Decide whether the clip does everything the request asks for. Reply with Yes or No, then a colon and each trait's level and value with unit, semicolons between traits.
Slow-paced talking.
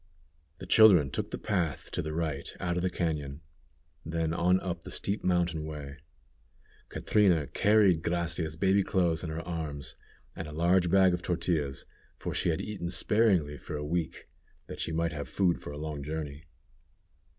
No: average, 175 wpm